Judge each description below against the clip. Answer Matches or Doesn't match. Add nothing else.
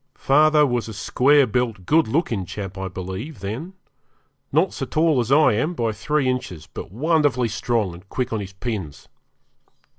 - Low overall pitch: Matches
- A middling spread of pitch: Doesn't match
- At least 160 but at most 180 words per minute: Matches